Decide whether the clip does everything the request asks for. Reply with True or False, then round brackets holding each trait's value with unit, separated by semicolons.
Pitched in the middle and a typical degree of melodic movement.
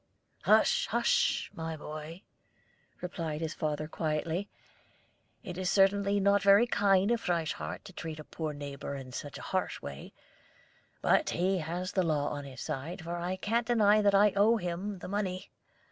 True (180 Hz; 4.5 semitones)